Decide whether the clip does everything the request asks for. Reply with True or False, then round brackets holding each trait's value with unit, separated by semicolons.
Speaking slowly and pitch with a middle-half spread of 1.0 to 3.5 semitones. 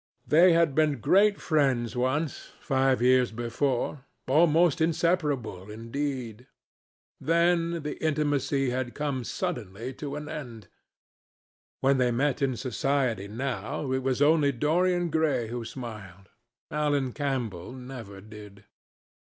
False (115 wpm; 4.1 semitones)